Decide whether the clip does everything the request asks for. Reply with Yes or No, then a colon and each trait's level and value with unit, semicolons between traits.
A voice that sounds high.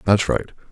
No: very low, 90 Hz